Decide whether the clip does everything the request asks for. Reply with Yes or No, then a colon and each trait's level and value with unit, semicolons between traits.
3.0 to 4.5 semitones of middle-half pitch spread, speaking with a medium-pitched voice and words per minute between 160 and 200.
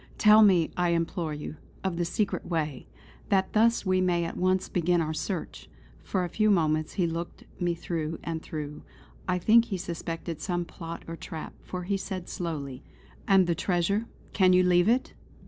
No: narrow, 2.4 semitones; medium, 175 Hz; average, 180 wpm